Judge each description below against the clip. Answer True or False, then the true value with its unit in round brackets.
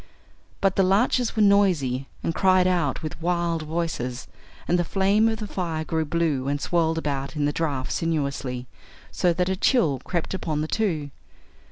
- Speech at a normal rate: True (175 wpm)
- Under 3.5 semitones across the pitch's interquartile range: False (4.2 semitones)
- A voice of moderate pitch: True (165 Hz)